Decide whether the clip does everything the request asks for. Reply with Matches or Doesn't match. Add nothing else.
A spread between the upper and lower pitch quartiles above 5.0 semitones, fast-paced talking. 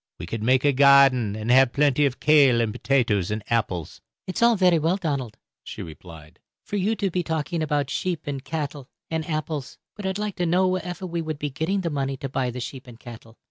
Matches